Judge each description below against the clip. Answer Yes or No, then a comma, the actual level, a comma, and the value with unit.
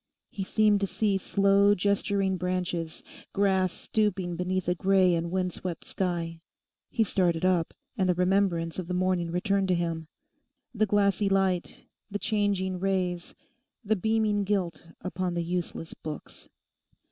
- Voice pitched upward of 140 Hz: Yes, medium, 185 Hz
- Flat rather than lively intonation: Yes, narrow, 2.3 semitones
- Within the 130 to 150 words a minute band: Yes, average, 140 wpm